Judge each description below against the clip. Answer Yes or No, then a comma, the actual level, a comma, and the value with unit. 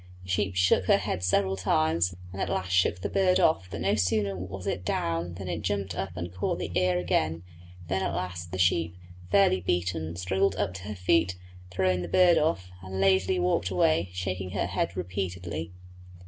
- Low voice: Yes, very low, 90 Hz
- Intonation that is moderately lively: No, narrow, 1.4 semitones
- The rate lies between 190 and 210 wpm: Yes, average, 195 wpm